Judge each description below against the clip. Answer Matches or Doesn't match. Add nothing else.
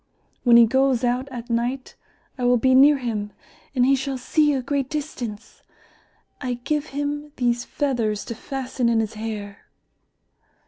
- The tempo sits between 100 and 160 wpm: Matches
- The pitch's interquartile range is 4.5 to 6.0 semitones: Doesn't match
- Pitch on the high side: Matches